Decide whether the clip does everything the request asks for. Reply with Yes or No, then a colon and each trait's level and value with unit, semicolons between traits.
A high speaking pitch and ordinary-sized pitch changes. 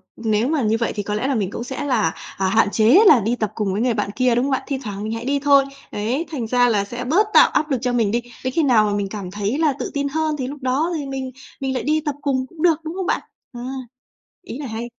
Yes: very high, 250 Hz; average, 4.5 semitones